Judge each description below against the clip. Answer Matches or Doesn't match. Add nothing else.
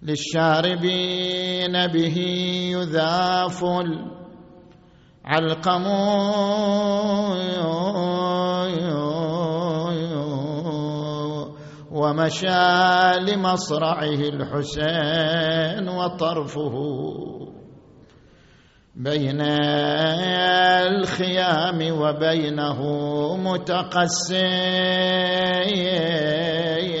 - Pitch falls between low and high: Matches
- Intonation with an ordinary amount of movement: Matches